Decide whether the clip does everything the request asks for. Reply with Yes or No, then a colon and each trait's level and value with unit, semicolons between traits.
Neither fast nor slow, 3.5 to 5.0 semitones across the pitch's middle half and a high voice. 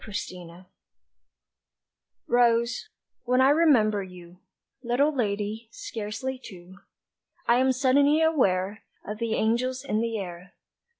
No: slow, 115 wpm; average, 4.4 semitones; high, 230 Hz